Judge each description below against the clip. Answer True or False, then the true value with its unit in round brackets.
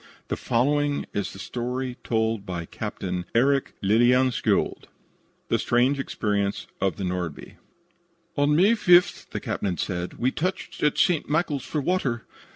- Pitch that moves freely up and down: True (6.4 semitones)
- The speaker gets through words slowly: False (145 wpm)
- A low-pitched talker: True (125 Hz)